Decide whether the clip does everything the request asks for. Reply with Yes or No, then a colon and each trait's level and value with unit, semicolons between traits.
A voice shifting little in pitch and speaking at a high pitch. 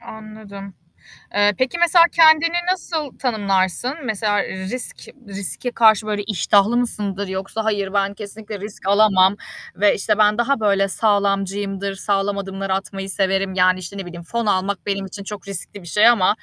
Yes: narrow, 2.0 semitones; high, 200 Hz